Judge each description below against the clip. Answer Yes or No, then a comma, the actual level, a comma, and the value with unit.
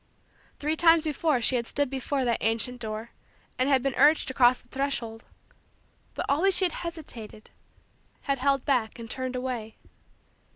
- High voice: Yes, very high, 260 Hz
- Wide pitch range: No, average, 3.4 semitones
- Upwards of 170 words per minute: No, average, 165 wpm